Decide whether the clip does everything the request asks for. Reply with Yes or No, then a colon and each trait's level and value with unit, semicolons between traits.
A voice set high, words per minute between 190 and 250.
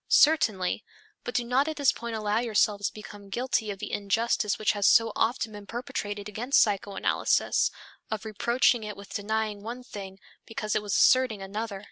No: high, 215 Hz; average, 175 wpm